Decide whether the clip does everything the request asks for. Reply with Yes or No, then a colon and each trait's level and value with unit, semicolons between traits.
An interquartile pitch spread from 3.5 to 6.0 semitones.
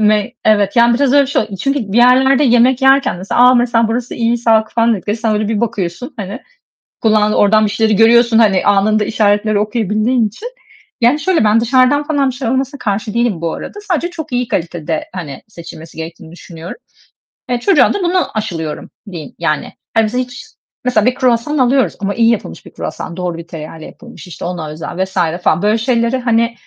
Yes: average, 3.8 semitones